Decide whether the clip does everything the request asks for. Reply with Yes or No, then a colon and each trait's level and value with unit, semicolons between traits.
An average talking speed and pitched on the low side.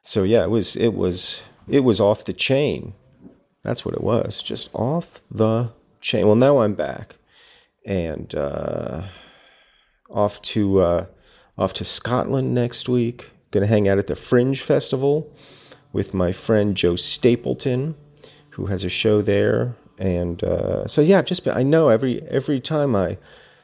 Yes: average, 160 wpm; low, 115 Hz